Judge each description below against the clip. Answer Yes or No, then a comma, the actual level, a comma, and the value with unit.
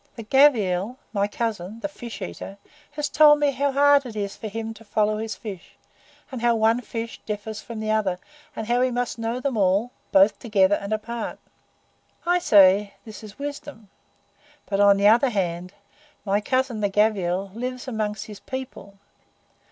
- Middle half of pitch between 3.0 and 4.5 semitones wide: Yes, average, 3.5 semitones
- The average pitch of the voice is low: No, high, 220 Hz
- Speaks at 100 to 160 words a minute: No, average, 175 wpm